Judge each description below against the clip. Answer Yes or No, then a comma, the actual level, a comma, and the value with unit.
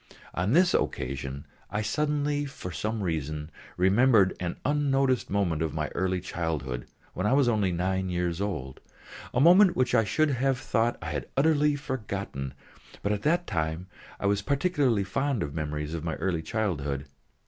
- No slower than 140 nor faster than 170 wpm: Yes, average, 165 wpm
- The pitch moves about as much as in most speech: No, wide, 8.7 semitones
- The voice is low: Yes, low, 100 Hz